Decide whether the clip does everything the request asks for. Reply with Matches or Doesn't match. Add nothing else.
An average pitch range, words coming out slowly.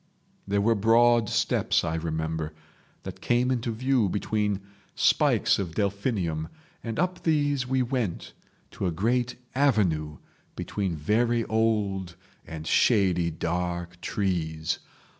Doesn't match